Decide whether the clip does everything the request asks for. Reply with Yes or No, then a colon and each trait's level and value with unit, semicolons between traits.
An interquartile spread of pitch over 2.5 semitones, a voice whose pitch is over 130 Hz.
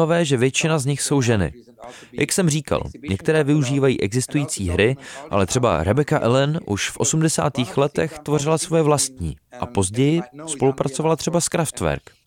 Yes: average, 5.2 semitones; medium, 140 Hz